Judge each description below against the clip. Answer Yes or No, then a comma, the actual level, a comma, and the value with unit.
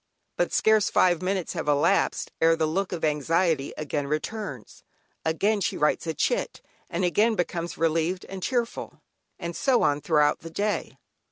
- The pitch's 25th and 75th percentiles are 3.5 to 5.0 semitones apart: Yes, average, 3.9 semitones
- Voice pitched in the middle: Yes, medium, 170 Hz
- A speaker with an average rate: Yes, average, 160 wpm